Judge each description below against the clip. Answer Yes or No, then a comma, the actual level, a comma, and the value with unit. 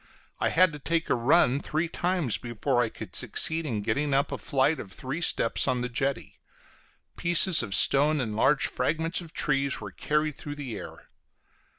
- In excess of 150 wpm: Yes, average, 185 wpm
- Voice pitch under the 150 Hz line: Yes, medium, 140 Hz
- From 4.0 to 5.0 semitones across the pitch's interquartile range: Yes, average, 4.5 semitones